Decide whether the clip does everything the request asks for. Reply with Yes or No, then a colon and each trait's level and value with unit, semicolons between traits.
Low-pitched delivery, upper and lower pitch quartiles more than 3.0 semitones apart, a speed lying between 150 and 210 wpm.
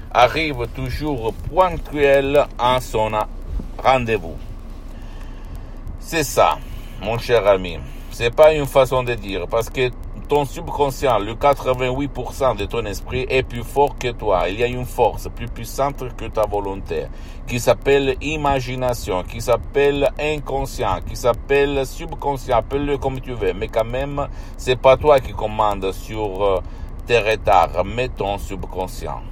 No: low, 125 Hz; average, 4.4 semitones; average, 140 wpm